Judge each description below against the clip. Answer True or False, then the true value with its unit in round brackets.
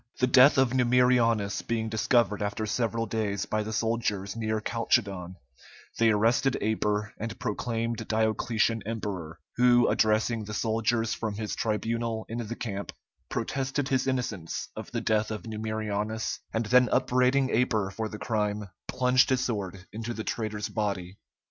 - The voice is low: True (110 Hz)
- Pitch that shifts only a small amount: True (2.1 semitones)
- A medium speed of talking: True (150 wpm)